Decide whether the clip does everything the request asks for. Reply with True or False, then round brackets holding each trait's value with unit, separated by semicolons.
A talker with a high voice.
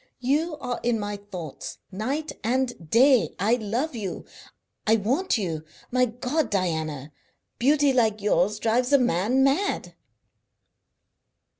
True (235 Hz)